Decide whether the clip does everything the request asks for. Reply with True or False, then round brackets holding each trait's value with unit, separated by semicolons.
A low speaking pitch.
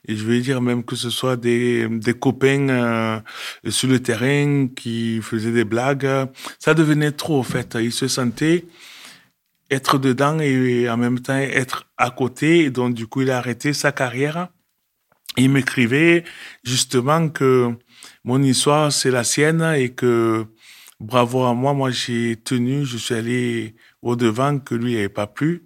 True (130 Hz)